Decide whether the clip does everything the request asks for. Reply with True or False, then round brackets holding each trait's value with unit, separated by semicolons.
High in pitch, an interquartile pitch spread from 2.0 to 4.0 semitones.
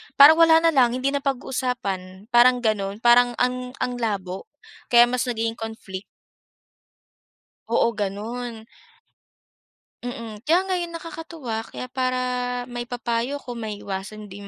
True (240 Hz; 2.9 semitones)